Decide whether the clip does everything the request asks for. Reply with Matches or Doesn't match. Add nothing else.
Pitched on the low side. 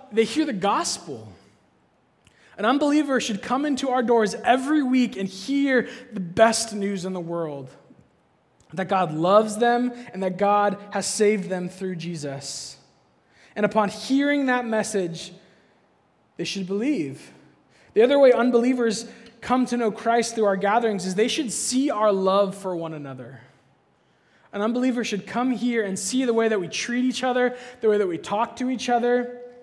Doesn't match